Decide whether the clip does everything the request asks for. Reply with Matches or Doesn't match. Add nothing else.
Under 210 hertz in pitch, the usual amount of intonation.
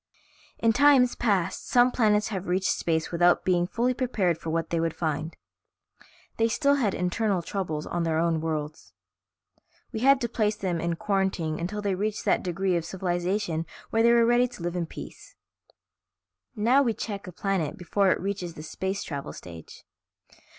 Matches